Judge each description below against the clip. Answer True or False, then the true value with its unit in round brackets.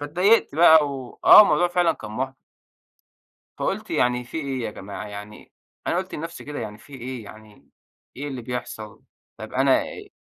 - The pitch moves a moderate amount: False (6.5 semitones)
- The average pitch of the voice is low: True (130 Hz)